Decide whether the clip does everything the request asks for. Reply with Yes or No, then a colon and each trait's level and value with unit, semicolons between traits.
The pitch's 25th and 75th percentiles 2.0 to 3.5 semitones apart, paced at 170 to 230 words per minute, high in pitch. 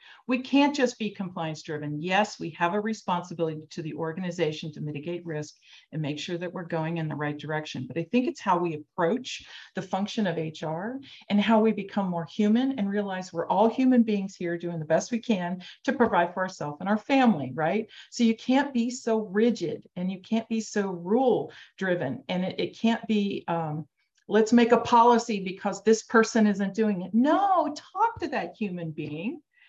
No: average, 5.3 semitones; average, 200 wpm; high, 200 Hz